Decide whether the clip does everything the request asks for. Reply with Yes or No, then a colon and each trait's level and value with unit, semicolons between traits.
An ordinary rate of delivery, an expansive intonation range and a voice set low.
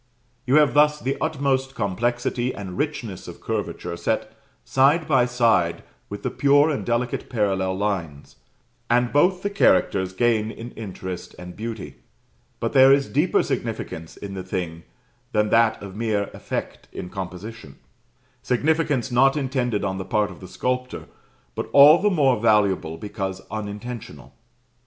Yes: average, 145 wpm; wide, 5.7 semitones; low, 115 Hz